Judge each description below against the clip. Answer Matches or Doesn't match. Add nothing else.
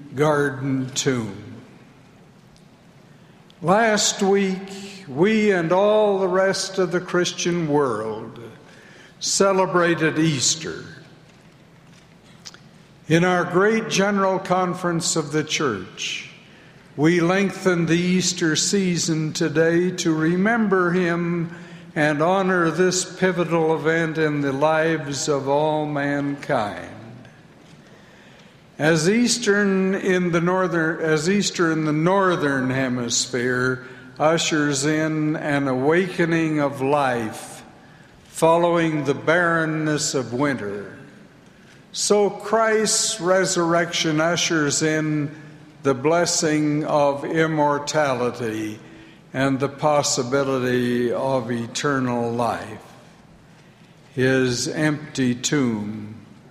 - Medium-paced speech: Doesn't match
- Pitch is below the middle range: Doesn't match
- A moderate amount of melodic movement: Matches